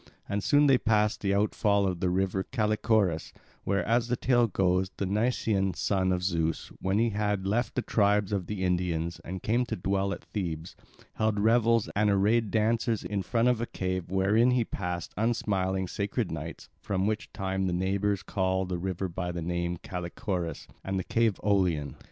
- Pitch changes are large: No, average, 2.8 semitones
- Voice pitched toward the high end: No, low, 100 Hz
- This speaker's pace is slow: No, average, 185 wpm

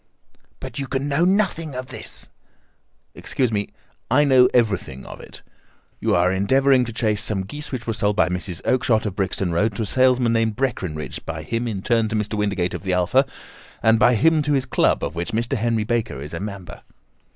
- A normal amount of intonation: Yes, average, 4.6 semitones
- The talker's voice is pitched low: Yes, low, 115 Hz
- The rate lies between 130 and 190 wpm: No, fast, 205 wpm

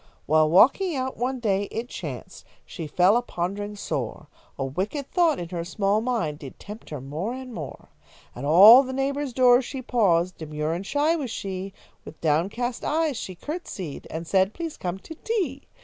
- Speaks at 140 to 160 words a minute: No, average, 180 wpm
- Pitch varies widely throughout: Yes, wide, 7.5 semitones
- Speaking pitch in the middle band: No, high, 205 Hz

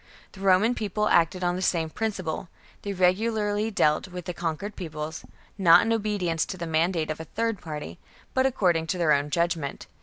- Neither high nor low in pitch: Yes, medium, 180 Hz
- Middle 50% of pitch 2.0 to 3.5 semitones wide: No, average, 4.2 semitones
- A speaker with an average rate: Yes, average, 190 wpm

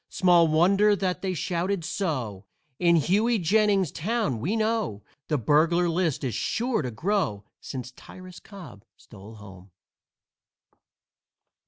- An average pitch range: No, wide, 7.6 semitones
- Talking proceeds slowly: Yes, slow, 125 wpm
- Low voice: No, medium, 170 Hz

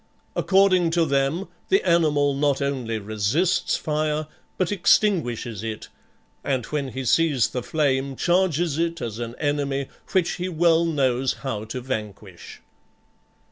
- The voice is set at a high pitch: No, medium, 140 Hz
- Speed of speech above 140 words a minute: No, slow, 135 wpm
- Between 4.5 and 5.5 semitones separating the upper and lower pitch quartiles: Yes, average, 5.1 semitones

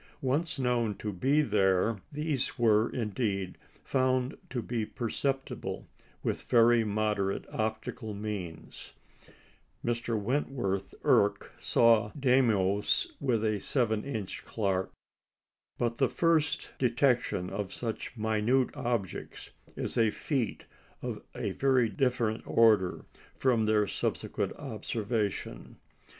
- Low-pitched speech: Yes, low, 115 Hz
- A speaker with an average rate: No, slow, 110 wpm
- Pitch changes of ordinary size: Yes, average, 3.4 semitones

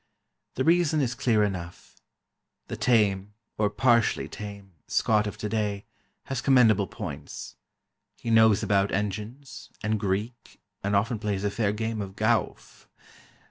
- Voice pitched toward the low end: Yes, low, 105 Hz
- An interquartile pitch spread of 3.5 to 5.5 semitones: No, narrow, 2.6 semitones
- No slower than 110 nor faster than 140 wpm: Yes, slow, 135 wpm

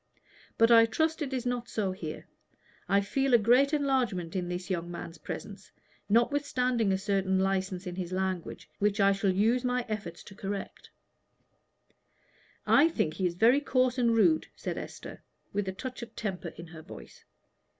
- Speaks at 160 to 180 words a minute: Yes, average, 170 wpm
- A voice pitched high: Yes, high, 205 Hz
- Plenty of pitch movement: No, average, 4.9 semitones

